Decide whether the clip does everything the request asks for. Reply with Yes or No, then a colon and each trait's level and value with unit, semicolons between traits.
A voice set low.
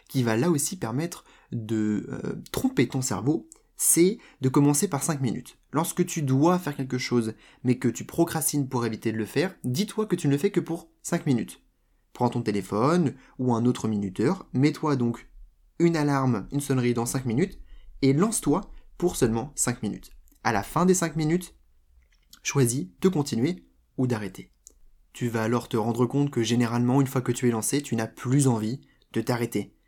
Yes: low, 130 Hz